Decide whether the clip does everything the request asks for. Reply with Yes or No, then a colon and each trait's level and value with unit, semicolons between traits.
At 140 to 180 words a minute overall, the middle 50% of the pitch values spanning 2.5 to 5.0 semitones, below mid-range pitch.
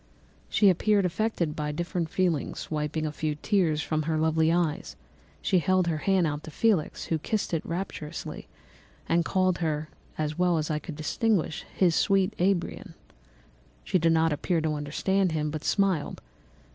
No: average, 165 wpm; average, 3.3 semitones; medium, 165 Hz